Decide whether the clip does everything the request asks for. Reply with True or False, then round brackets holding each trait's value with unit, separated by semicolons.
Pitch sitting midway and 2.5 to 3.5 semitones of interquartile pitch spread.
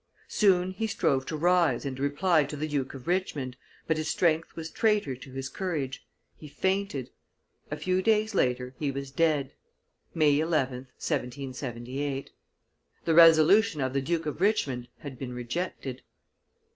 False (150 Hz; 4.8 semitones)